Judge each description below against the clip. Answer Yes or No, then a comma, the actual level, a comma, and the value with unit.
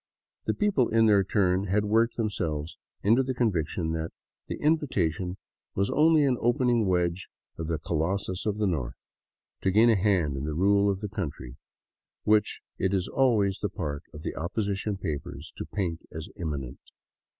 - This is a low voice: Yes, very low, 95 Hz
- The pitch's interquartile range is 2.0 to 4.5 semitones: No, average, 5.0 semitones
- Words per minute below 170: No, average, 180 wpm